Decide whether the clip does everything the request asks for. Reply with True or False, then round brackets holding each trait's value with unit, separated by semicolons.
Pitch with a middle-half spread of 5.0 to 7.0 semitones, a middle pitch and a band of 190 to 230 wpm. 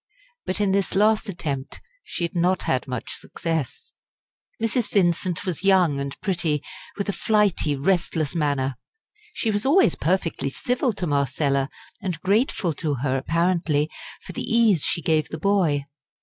False (5.5 semitones; 170 Hz; 150 wpm)